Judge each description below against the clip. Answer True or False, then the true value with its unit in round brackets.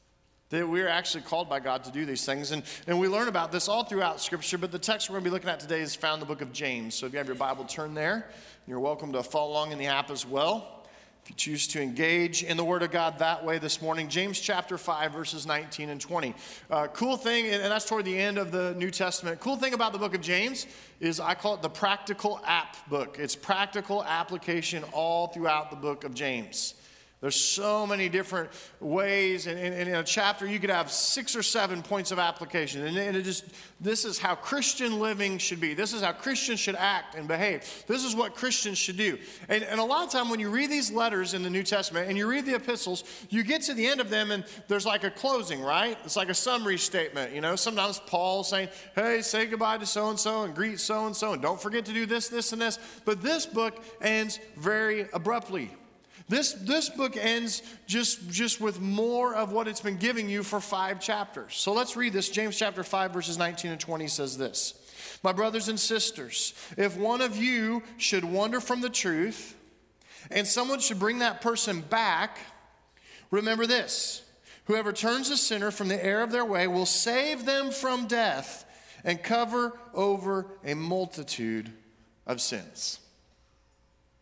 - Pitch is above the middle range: True (195 Hz)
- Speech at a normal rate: False (210 wpm)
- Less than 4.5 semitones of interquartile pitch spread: False (4.9 semitones)